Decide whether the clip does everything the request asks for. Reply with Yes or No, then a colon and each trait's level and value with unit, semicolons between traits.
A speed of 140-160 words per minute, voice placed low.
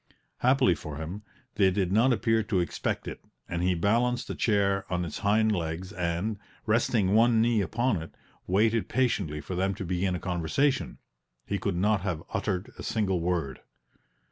No: average, 170 wpm; low, 100 Hz